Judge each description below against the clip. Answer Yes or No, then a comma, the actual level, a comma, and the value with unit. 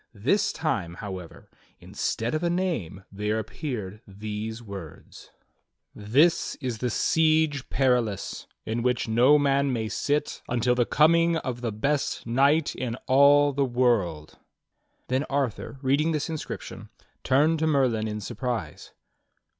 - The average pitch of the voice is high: No, low, 125 Hz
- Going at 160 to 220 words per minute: No, average, 150 wpm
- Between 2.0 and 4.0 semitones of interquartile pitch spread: No, average, 4.9 semitones